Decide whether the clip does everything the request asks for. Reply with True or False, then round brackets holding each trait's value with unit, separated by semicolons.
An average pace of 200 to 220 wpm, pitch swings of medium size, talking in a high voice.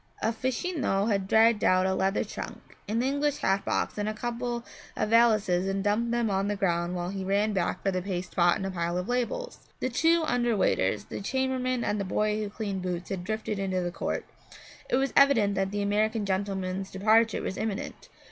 True (205 wpm; 3.6 semitones; 205 Hz)